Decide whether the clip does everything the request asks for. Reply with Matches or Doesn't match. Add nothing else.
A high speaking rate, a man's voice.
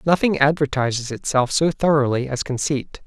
Doesn't match